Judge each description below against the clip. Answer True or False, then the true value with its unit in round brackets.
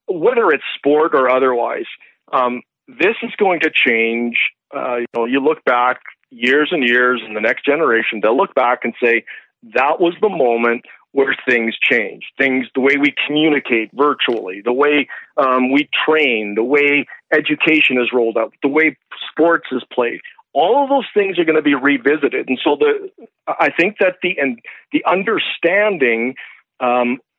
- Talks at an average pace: True (170 wpm)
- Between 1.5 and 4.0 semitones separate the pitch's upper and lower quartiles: False (4.6 semitones)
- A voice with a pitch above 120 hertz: True (140 Hz)